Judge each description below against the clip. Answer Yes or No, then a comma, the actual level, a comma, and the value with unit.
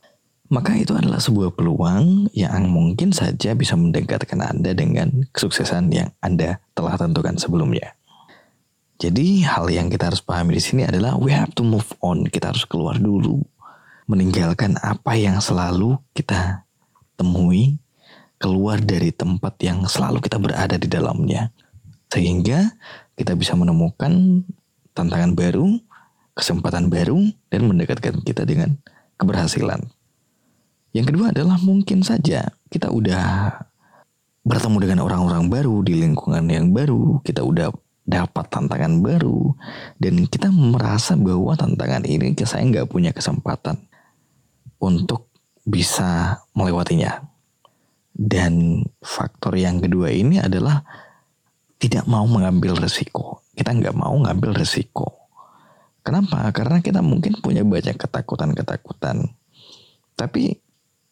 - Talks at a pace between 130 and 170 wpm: No, average, 120 wpm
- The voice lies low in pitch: Yes, low, 120 Hz